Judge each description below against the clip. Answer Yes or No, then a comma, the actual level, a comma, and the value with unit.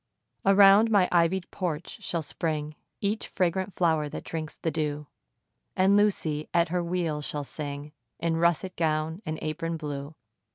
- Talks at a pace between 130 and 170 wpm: Yes, average, 150 wpm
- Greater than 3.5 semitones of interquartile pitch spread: No, average, 3.1 semitones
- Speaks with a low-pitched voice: No, medium, 165 Hz